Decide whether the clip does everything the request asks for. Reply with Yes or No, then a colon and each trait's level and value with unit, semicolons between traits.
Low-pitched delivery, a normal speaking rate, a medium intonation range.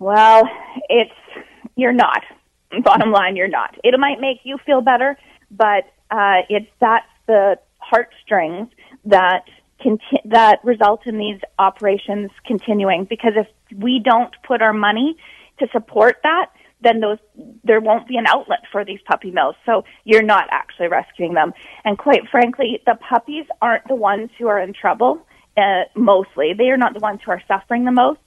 No: high, 225 Hz; average, 170 wpm; average, 3.3 semitones